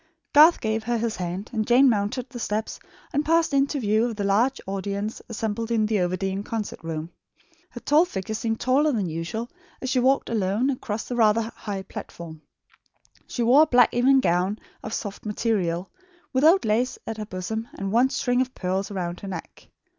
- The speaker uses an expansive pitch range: No, average, 4.0 semitones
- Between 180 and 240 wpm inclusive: Yes, average, 190 wpm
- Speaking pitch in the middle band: No, high, 220 Hz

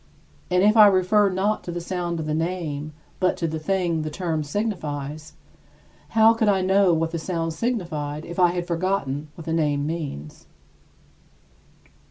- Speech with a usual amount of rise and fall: Yes, average, 3.5 semitones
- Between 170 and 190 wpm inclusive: Yes, average, 175 wpm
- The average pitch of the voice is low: No, medium, 170 Hz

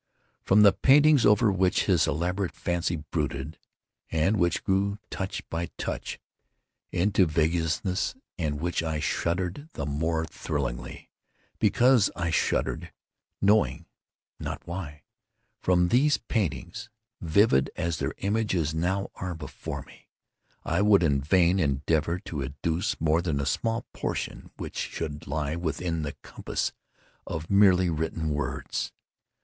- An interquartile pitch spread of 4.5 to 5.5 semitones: No, average, 4.0 semitones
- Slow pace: Yes, slow, 125 wpm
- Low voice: Yes, very low, 85 Hz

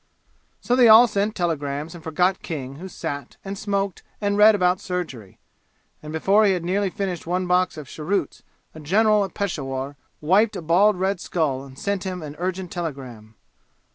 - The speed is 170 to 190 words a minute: Yes, average, 175 wpm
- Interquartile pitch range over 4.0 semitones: Yes, average, 4.7 semitones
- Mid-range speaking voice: Yes, medium, 180 Hz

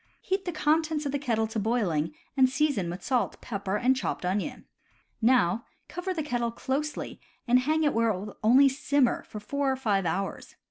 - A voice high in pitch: Yes, very high, 250 Hz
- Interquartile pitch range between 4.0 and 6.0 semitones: Yes, average, 5.3 semitones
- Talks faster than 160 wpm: Yes, average, 190 wpm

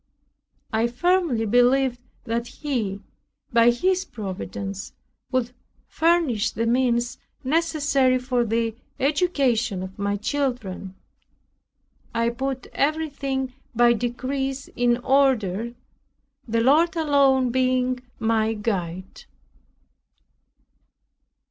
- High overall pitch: Yes, high, 245 Hz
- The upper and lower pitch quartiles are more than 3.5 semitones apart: No, average, 3.2 semitones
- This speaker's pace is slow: Yes, slow, 90 wpm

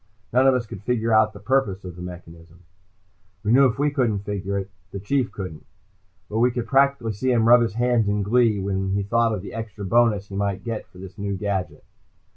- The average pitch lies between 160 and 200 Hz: No, low, 105 Hz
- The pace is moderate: No, fast, 225 wpm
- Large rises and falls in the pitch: No, average, 3.6 semitones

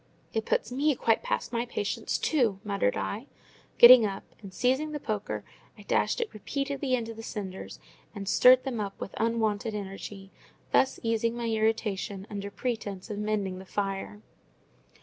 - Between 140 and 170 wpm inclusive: Yes, average, 160 wpm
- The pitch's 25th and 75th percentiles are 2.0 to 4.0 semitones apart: Yes, average, 3.4 semitones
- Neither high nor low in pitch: No, high, 220 Hz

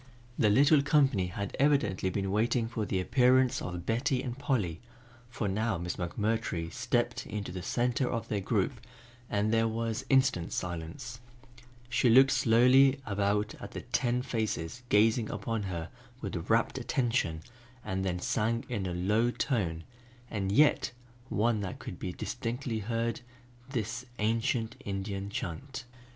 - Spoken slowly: No, average, 145 wpm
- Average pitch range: Yes, average, 4.1 semitones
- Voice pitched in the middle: No, low, 115 Hz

